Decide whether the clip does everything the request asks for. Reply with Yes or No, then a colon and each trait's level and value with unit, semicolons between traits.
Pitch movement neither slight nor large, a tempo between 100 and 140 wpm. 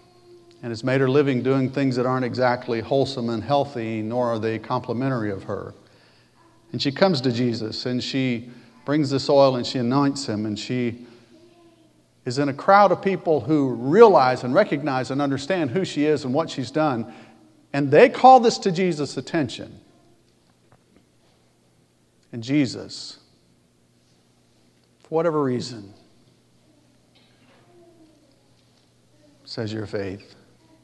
Yes: average, 4.3 semitones; slow, 135 wpm